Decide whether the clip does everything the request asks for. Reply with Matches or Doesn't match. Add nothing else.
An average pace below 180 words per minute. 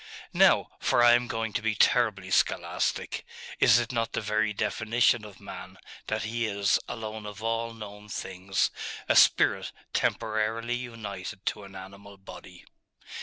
Matches